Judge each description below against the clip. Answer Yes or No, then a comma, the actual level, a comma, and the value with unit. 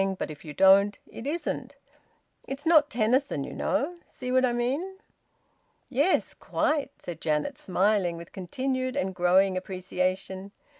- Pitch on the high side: Yes, high, 205 Hz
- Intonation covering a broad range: Yes, wide, 6.5 semitones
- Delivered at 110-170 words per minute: Yes, average, 140 wpm